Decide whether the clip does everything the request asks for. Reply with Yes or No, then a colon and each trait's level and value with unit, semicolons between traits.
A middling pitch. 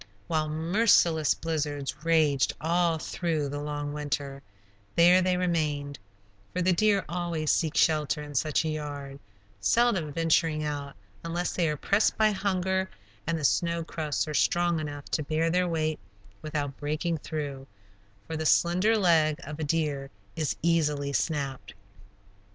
Yes: medium, 155 Hz